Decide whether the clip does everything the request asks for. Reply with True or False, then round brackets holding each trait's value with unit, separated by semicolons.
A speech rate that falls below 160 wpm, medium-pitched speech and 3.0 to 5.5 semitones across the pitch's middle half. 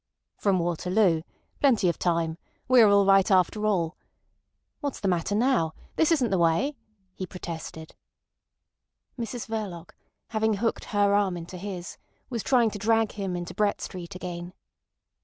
False (150 wpm; 195 Hz; 4.0 semitones)